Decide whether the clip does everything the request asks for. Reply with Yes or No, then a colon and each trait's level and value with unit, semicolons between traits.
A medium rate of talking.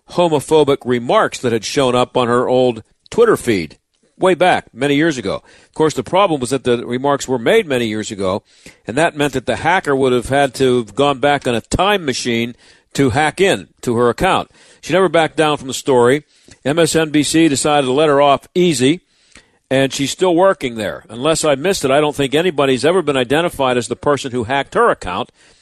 No: fast, 210 wpm